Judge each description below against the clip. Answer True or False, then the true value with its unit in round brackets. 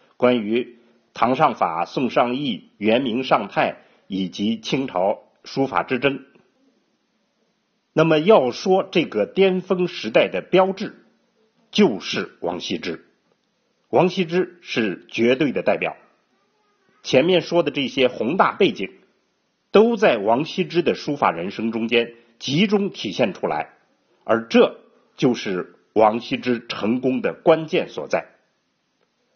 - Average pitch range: False (7.2 semitones)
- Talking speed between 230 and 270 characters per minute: False (180 characters per minute)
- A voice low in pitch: False (160 Hz)